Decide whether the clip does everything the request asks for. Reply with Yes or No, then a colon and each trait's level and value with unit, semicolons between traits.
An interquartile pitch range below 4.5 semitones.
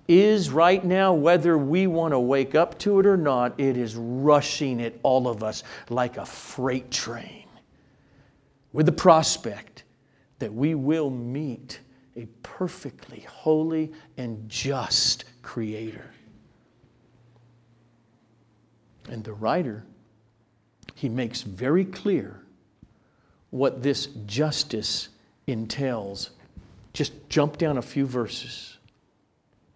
No: average, 5.0 semitones